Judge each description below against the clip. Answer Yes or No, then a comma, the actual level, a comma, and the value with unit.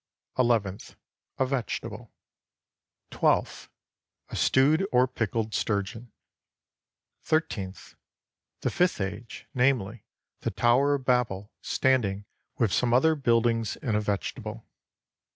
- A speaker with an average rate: No, slow, 100 wpm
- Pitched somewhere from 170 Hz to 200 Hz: No, low, 120 Hz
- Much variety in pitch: No, average, 3.7 semitones